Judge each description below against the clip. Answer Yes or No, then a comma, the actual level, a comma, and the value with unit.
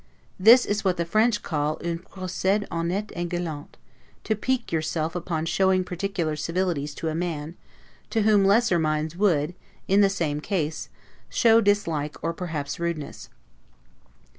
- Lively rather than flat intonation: No, average, 4.0 semitones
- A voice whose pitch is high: No, medium, 175 Hz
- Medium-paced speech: Yes, average, 145 wpm